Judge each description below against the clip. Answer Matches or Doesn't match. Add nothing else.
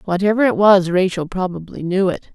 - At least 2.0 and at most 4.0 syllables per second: Doesn't match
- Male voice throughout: Doesn't match